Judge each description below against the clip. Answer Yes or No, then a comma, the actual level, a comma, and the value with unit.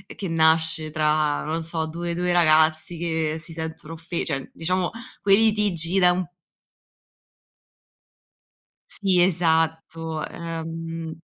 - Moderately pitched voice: Yes, medium, 165 Hz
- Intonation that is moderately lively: No, narrow, 1.6 semitones